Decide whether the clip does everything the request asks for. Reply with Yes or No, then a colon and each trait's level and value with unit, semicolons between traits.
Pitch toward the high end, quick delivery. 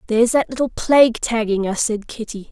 No: high, 230 Hz; average, 190 wpm